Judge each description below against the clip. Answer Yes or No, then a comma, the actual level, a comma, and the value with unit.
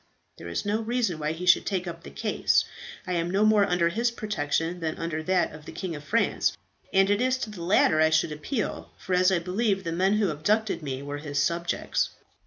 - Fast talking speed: Yes, fast, 225 wpm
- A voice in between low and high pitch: Yes, medium, 180 Hz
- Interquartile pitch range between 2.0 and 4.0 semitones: No, average, 4.5 semitones